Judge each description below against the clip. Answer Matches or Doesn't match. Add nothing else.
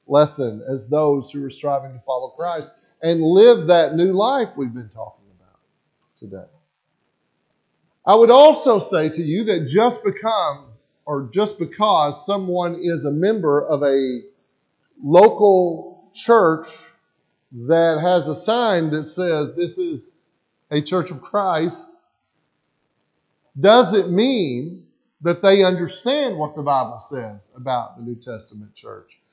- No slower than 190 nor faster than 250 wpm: Doesn't match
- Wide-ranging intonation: Matches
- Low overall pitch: Doesn't match